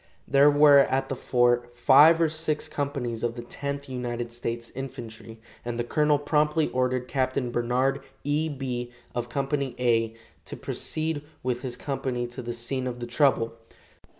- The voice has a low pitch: Yes, low, 130 Hz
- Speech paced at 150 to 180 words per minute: Yes, average, 160 wpm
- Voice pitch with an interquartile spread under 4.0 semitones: Yes, average, 2.8 semitones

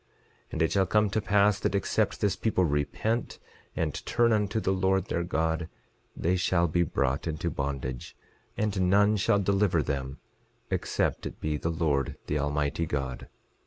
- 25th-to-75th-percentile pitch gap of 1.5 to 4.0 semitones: No, average, 5.3 semitones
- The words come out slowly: No, average, 165 wpm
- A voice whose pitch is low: Yes, very low, 85 Hz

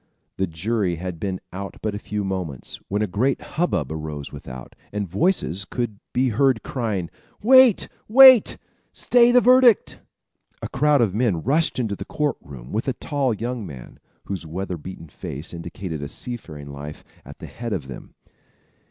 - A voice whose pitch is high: No, low, 100 Hz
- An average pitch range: No, wide, 7.8 semitones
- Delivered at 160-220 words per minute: Yes, average, 170 wpm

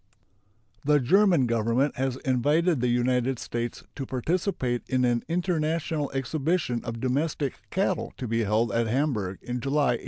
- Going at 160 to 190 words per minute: No, average, 150 wpm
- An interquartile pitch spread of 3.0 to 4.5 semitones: Yes, average, 4.0 semitones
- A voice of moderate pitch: No, low, 130 Hz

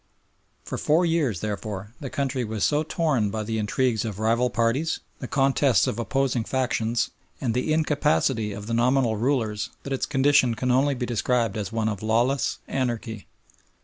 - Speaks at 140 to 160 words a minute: No, average, 170 wpm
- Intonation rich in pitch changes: No, average, 3.7 semitones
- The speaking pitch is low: Yes, low, 120 Hz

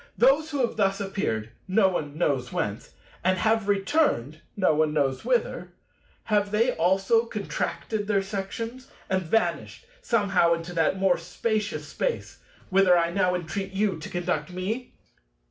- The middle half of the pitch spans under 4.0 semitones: No, average, 4.3 semitones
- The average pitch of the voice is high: Yes, high, 195 Hz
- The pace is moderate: No, slow, 130 wpm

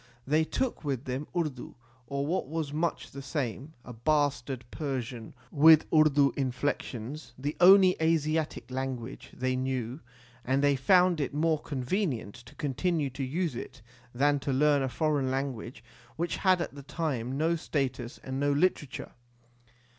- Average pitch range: Yes, average, 3.3 semitones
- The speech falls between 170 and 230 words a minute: No, average, 155 wpm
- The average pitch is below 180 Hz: Yes, medium, 140 Hz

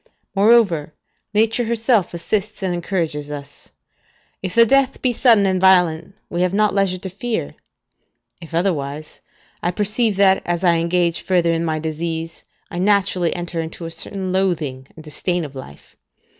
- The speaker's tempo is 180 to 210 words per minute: No, average, 155 wpm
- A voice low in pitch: No, medium, 180 Hz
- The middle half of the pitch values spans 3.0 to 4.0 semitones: Yes, average, 3.5 semitones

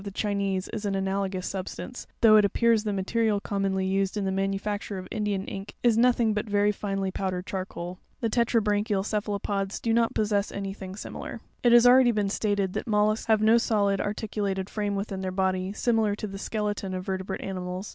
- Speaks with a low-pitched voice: No, high, 200 Hz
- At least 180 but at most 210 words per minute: Yes, average, 200 wpm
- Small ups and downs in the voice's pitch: Yes, narrow, 1.8 semitones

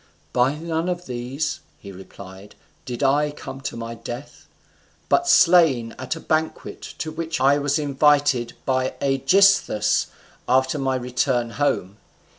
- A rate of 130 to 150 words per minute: Yes, slow, 135 wpm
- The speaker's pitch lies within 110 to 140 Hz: Yes, low, 135 Hz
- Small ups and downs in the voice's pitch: No, average, 4.2 semitones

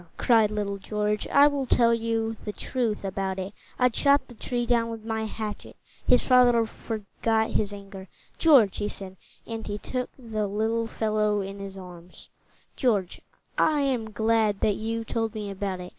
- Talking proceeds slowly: No, average, 175 wpm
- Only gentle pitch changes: Yes, narrow, 2.3 semitones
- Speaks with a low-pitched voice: No, high, 220 Hz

